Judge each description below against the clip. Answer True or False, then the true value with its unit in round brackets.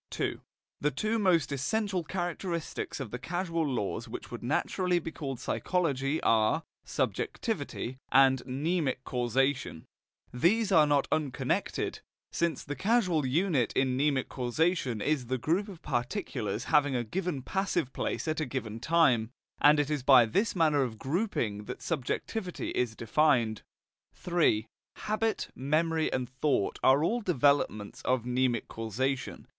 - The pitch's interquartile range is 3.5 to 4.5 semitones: False (5.3 semitones)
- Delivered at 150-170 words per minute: False (140 wpm)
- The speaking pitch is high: False (140 Hz)